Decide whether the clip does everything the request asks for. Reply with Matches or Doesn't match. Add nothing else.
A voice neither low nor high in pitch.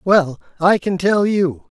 Matches